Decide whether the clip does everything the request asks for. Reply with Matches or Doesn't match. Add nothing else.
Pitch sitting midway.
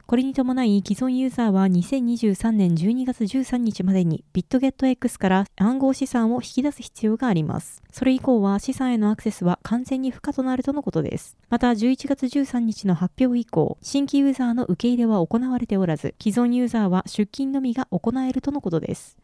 Doesn't match